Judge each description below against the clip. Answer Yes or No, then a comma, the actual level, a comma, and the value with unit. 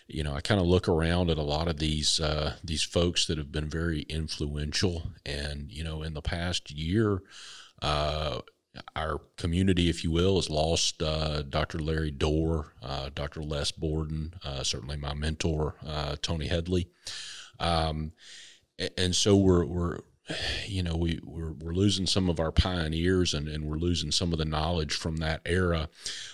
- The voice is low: Yes, very low, 80 Hz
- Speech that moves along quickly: No, average, 175 wpm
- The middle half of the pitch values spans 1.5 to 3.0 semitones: Yes, narrow, 2.4 semitones